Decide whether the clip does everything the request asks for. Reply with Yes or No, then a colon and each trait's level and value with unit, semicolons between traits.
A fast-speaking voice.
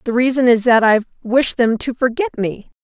Yes: fast, 210 wpm